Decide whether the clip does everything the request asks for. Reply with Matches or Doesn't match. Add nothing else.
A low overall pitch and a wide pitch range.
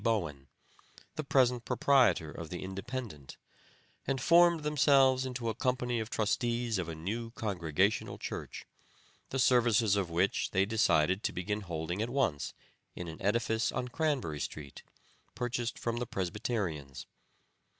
Matches